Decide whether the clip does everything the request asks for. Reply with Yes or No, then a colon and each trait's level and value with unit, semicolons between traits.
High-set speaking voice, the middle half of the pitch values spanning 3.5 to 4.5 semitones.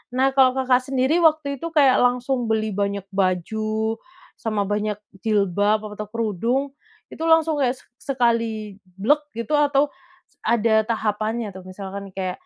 Yes: high, 225 Hz; average, 4.1 semitones